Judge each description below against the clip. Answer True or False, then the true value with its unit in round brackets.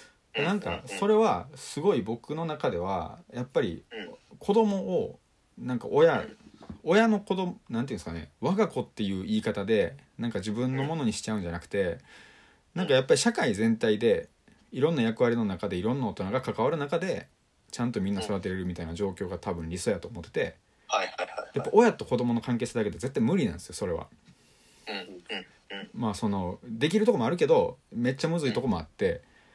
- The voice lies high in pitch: False (130 Hz)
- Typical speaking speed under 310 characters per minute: False (370 characters per minute)